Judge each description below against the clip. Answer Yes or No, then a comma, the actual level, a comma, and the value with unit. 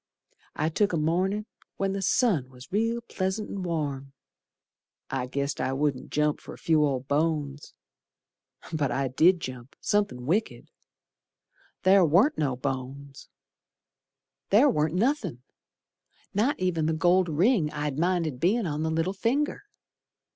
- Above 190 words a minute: No, average, 140 wpm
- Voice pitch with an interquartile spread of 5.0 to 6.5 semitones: Yes, wide, 5.5 semitones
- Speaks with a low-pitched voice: No, medium, 160 Hz